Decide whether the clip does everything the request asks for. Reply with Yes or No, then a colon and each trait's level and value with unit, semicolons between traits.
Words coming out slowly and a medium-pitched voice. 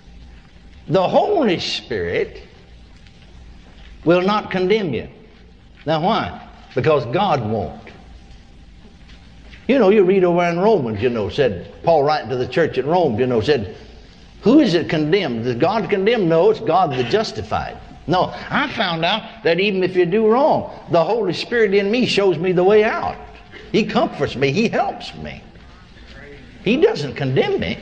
No: average, 160 wpm; medium, 180 Hz